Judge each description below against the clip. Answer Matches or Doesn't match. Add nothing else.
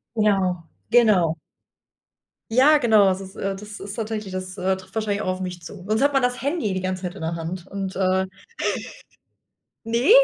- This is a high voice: Matches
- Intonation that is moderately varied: Matches